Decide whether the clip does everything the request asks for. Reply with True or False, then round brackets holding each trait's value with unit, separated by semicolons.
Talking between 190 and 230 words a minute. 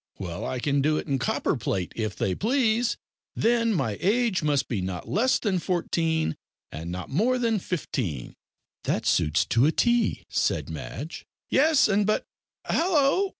False (155 wpm)